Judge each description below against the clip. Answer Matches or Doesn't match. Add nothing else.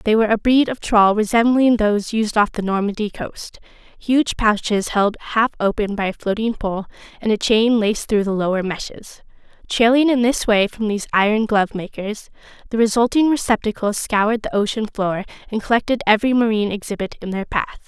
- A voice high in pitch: Matches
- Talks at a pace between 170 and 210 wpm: Matches